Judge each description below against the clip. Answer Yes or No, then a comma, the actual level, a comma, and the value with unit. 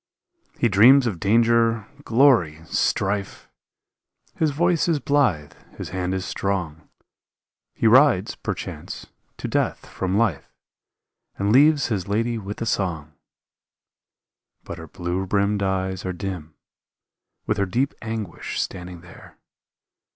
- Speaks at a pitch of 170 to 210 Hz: No, low, 100 Hz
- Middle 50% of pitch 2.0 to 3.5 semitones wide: No, average, 4.5 semitones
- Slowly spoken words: Yes, slow, 120 wpm